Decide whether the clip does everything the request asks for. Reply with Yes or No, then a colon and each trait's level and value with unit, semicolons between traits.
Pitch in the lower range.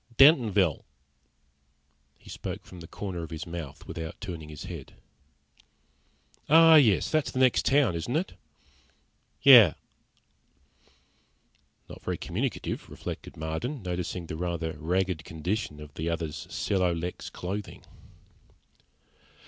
Yes: very low, 90 Hz